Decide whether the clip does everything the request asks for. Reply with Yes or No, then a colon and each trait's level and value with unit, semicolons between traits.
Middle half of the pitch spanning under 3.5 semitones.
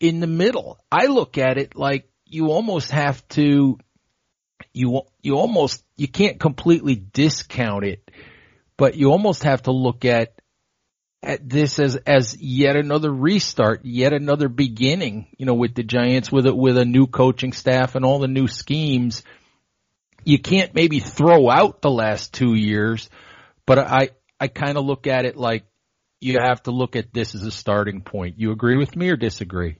Yes: average, 3.1 semitones